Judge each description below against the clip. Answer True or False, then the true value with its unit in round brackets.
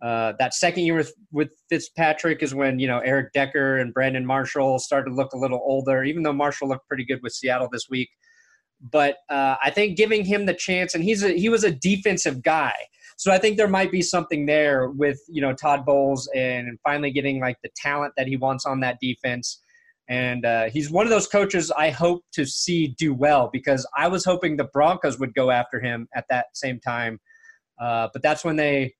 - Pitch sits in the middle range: True (145 Hz)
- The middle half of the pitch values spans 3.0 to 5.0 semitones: True (4.6 semitones)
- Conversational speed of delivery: False (215 wpm)